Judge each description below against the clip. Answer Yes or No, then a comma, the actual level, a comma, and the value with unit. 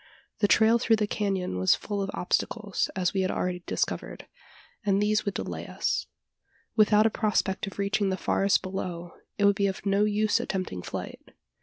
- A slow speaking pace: No, average, 180 wpm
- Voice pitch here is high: Yes, high, 200 Hz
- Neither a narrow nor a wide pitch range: No, narrow, 1.9 semitones